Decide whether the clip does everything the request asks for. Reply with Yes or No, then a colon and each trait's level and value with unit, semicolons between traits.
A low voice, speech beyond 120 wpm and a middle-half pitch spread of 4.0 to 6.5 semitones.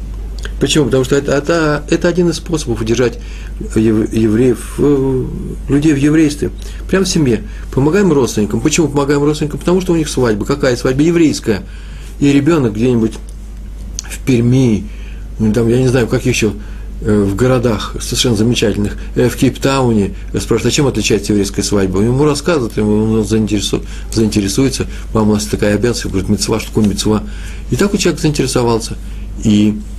Yes: low, 115 Hz; average, 155 wpm; average, 5.2 semitones